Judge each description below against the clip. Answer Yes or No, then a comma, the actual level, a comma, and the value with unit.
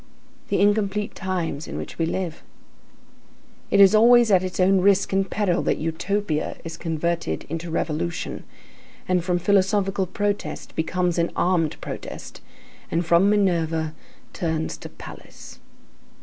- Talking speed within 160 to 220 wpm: No, slow, 135 wpm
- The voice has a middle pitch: Yes, medium, 180 Hz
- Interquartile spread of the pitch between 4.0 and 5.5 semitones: No, average, 3.2 semitones